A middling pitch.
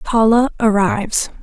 No: high, 220 Hz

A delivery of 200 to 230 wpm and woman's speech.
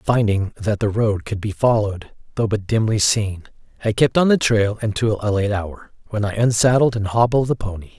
No: fast, 205 wpm; male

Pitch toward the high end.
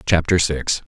No: very low, 80 Hz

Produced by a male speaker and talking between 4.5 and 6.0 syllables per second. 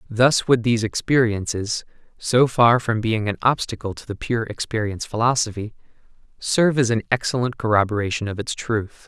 Yes: male; 5.3 syllables/s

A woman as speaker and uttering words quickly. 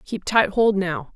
Yes: female; fast, 210 wpm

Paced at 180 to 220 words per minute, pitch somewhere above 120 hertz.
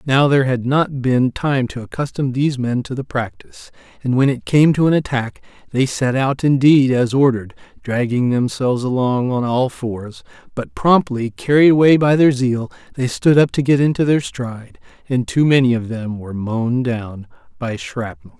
Yes: average, 185 wpm; low, 130 Hz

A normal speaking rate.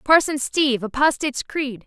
No: slow, 130 wpm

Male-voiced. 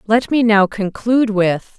No: female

